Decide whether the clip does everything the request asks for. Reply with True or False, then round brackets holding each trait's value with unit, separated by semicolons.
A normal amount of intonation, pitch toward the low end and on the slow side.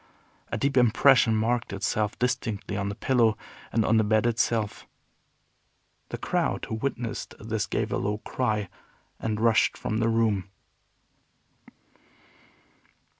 False (1.9 semitones; 110 Hz; 125 wpm)